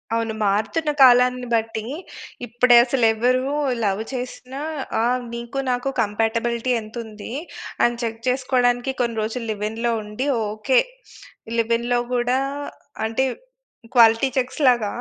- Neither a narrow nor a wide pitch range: No, narrow, 2.1 semitones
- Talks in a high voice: Yes, high, 235 Hz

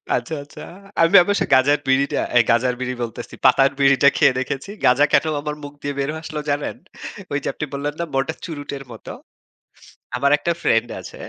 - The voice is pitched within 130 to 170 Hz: Yes, medium, 140 Hz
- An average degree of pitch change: No, narrow, 2.3 semitones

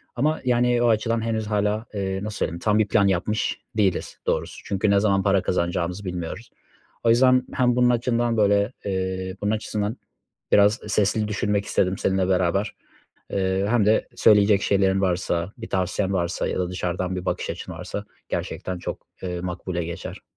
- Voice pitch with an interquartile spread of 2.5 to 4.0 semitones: Yes, average, 2.8 semitones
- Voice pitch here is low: Yes, low, 100 Hz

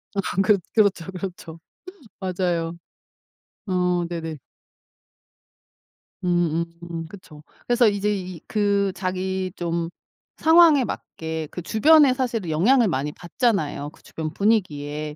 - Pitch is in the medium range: Yes, medium, 180 Hz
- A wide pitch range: No, average, 3.8 semitones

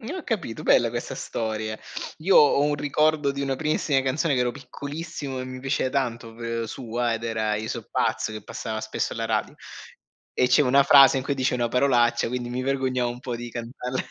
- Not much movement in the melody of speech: No, average, 3.1 semitones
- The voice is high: No, low, 130 Hz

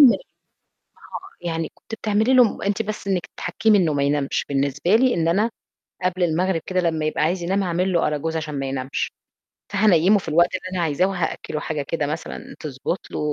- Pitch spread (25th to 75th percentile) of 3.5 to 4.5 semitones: Yes, average, 3.9 semitones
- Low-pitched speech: No, medium, 170 Hz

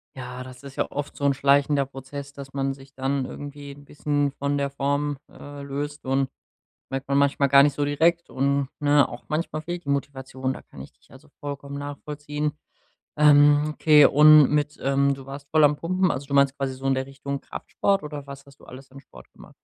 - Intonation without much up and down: Yes, narrow, 1.2 semitones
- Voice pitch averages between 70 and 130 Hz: No, medium, 140 Hz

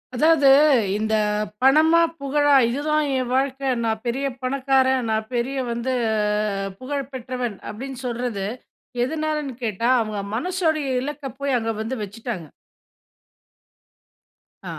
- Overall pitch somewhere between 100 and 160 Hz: No, very high, 260 Hz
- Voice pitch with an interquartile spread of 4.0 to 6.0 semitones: No, average, 3.3 semitones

